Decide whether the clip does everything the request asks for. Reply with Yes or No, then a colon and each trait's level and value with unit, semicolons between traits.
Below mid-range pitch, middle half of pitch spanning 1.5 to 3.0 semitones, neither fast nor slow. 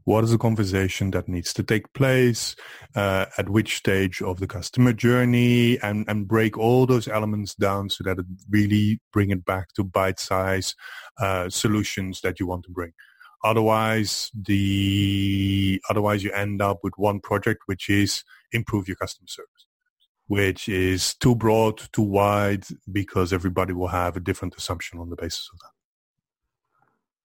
Yes: low, 100 Hz; narrow, 2.6 semitones; average, 165 wpm